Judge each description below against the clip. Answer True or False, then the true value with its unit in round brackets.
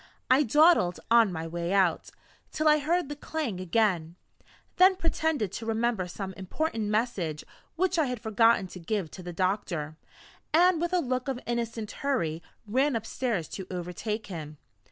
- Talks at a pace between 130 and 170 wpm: True (160 wpm)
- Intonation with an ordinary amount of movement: False (7.6 semitones)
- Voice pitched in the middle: False (220 Hz)